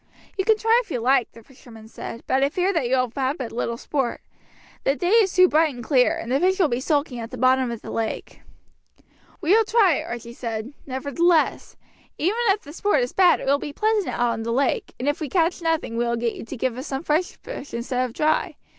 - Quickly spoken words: Yes, fast, 245 wpm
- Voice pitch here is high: Yes, very high, 275 Hz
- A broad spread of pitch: Yes, wide, 6.5 semitones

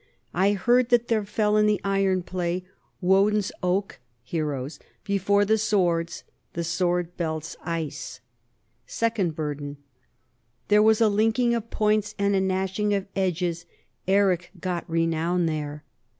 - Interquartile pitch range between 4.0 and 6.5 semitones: No, average, 3.6 semitones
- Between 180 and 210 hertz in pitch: Yes, high, 190 Hz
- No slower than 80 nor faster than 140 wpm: Yes, slow, 135 wpm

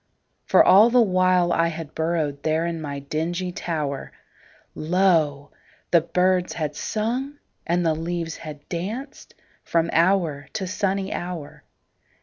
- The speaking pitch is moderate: Yes, medium, 170 Hz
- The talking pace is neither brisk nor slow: No, slow, 120 wpm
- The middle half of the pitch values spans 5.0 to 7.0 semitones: No, average, 2.9 semitones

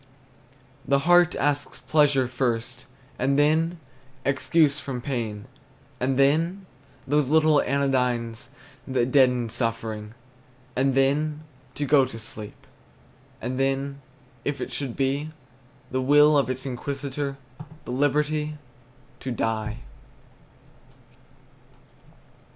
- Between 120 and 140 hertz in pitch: Yes, low, 135 Hz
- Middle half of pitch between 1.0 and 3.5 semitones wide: Yes, average, 2.7 semitones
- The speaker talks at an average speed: No, slow, 105 wpm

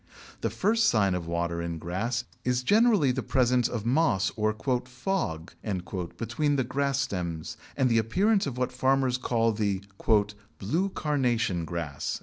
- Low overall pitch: Yes, low, 120 Hz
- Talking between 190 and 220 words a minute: No, average, 145 wpm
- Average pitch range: No, wide, 6.1 semitones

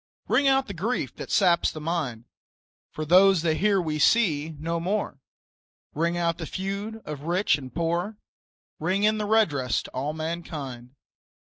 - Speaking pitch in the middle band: Yes, medium, 170 Hz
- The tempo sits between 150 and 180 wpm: Yes, average, 155 wpm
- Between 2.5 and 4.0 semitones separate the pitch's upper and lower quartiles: No, average, 4.6 semitones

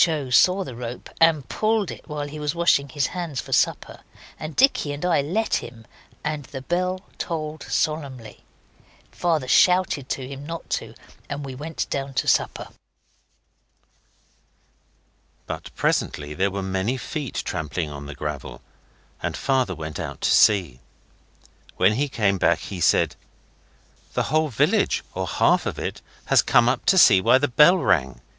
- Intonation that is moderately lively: No, wide, 7.1 semitones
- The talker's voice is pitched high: No, medium, 140 Hz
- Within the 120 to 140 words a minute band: No, average, 160 wpm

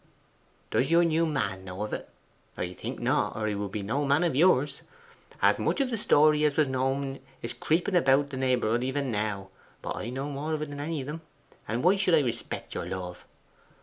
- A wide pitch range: Yes, wide, 5.8 semitones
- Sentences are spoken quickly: Yes, fast, 210 wpm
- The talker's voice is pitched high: No, low, 135 Hz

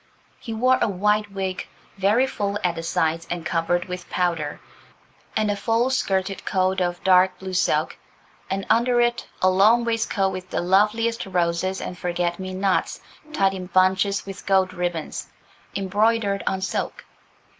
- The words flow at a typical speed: Yes, average, 155 wpm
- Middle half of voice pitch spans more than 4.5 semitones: No, narrow, 2.5 semitones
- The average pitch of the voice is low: No, high, 190 Hz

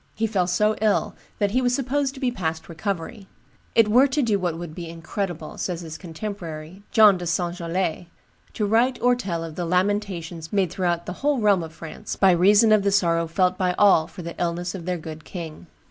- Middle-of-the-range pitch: Yes, medium, 180 Hz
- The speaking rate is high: Yes, fast, 210 wpm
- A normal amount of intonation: Yes, average, 3.9 semitones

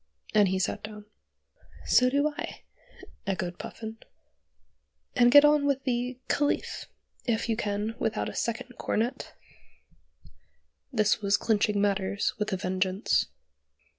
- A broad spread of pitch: No, average, 3.6 semitones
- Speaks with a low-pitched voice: No, high, 215 Hz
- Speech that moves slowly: Yes, slow, 125 wpm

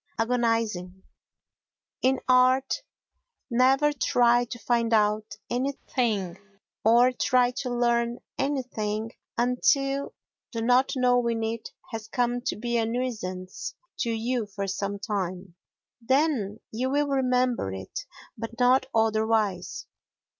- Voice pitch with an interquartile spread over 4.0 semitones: No, average, 2.8 semitones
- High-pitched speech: Yes, high, 235 Hz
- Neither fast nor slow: No, slow, 110 wpm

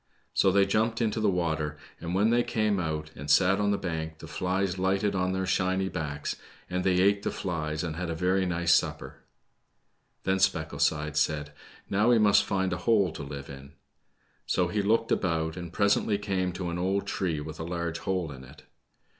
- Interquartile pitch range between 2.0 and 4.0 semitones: Yes, average, 3.5 semitones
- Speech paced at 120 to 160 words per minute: No, average, 195 wpm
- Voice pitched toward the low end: Yes, very low, 90 Hz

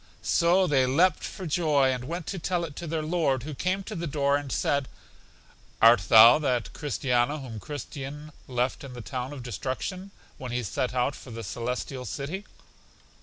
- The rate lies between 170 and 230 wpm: Yes, average, 180 wpm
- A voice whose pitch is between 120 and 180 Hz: Yes, medium, 140 Hz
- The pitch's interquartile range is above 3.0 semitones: Yes, average, 4.3 semitones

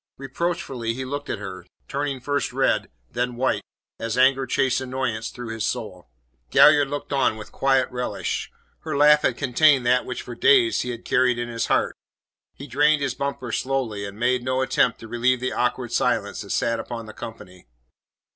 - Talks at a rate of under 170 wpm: No, average, 185 wpm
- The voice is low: Yes, low, 125 Hz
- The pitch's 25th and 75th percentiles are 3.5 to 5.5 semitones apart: No, average, 2.7 semitones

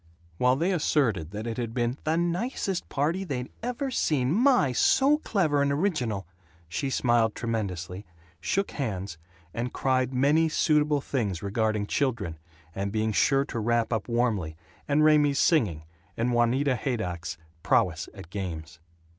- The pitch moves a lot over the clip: Yes, wide, 6.1 semitones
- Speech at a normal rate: Yes, average, 145 wpm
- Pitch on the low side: Yes, low, 125 Hz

